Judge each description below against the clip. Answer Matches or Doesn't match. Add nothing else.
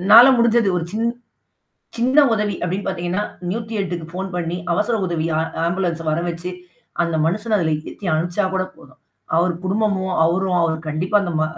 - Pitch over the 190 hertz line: Doesn't match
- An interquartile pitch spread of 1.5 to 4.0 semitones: Matches